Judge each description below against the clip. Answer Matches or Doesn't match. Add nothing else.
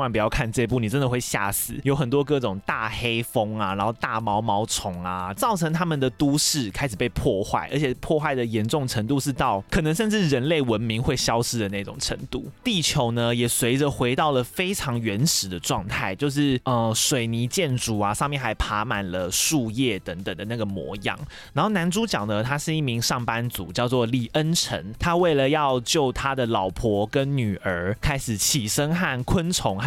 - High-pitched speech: Doesn't match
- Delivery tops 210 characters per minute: Matches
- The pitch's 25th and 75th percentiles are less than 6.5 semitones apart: Matches